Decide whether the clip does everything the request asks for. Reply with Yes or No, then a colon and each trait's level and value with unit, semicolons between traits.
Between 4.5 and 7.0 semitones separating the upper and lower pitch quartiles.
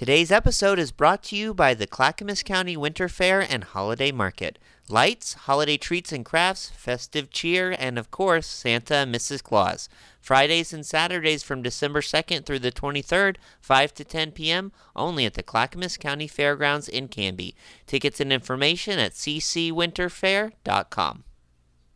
Yes: average, 5.1 semitones